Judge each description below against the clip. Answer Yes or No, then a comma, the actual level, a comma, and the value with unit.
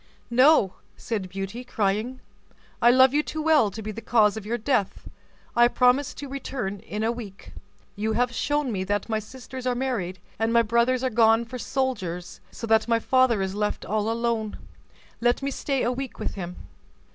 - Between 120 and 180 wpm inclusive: No, average, 190 wpm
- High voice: Yes, high, 235 Hz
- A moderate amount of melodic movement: Yes, average, 3.4 semitones